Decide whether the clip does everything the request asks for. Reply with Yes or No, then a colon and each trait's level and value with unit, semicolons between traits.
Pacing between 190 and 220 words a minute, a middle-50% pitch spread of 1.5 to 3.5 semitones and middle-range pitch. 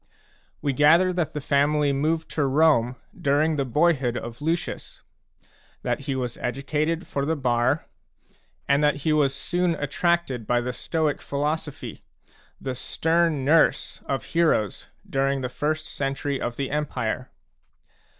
No: average, 140 wpm; average, 3.0 semitones; medium, 145 Hz